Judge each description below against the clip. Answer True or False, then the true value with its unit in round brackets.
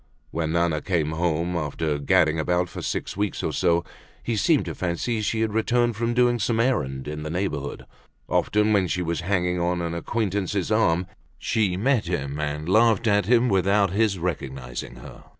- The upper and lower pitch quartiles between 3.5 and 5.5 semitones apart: True (4.9 semitones)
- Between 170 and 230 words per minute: True (180 wpm)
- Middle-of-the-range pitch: False (90 Hz)